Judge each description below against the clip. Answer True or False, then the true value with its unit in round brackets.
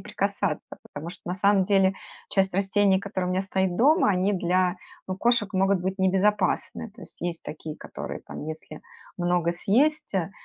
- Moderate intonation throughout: False (2.1 semitones)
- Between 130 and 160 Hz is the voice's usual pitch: False (190 Hz)